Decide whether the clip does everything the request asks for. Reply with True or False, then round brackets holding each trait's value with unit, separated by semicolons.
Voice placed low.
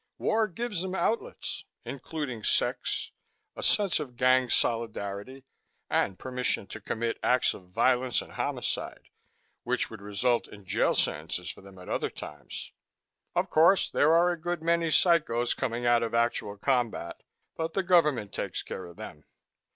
True (125 Hz)